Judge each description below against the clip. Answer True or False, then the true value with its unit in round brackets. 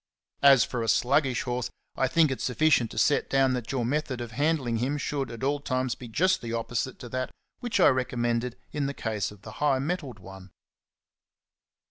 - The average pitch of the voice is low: True (130 Hz)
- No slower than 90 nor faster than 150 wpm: False (195 wpm)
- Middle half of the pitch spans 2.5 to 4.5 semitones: True (3.2 semitones)